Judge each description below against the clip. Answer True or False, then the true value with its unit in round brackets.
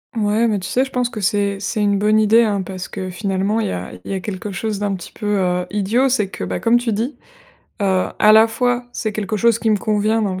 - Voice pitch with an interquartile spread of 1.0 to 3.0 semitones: True (2.6 semitones)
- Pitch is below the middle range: False (210 Hz)